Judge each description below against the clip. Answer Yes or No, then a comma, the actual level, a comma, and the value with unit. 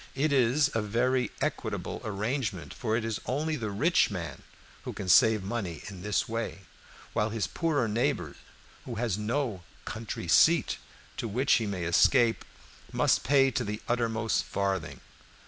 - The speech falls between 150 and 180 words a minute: Yes, average, 155 wpm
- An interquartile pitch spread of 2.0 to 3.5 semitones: No, average, 4.0 semitones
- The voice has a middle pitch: No, low, 115 Hz